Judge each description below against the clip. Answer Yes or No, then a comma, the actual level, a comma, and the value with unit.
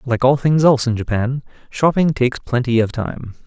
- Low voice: Yes, low, 130 Hz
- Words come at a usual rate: Yes, average, 190 wpm